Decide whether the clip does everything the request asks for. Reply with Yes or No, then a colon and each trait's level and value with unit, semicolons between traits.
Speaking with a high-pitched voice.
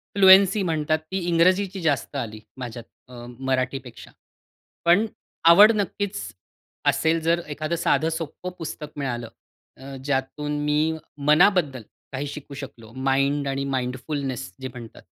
No: medium, 145 Hz